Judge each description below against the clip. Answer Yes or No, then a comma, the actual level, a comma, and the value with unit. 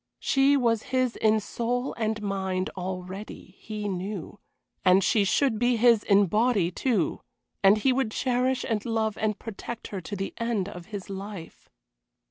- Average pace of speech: Yes, average, 160 wpm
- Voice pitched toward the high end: Yes, high, 215 Hz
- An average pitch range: Yes, average, 3.5 semitones